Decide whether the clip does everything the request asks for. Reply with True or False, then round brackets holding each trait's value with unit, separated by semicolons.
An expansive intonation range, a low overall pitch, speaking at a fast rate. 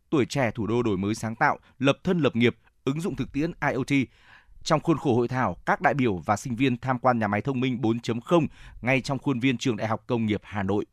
False (3.9 semitones; 125 Hz; 255 wpm)